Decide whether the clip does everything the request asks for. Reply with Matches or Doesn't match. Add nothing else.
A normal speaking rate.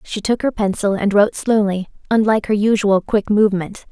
Matches